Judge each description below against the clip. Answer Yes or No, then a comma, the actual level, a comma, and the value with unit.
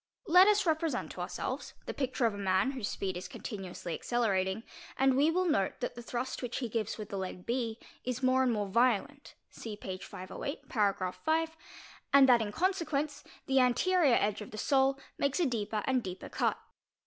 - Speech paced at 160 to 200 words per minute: Yes, average, 190 wpm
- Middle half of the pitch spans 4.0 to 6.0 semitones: Yes, wide, 5.4 semitones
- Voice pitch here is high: Yes, high, 245 Hz